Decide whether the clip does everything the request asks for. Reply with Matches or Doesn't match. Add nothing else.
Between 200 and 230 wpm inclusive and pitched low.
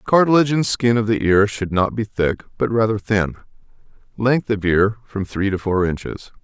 Matches